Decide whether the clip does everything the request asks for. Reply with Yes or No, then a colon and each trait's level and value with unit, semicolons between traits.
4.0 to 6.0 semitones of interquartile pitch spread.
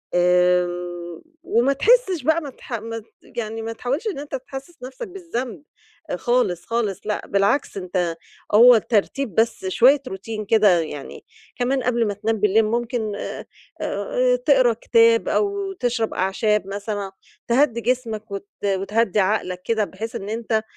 Yes: average, 5.0 semitones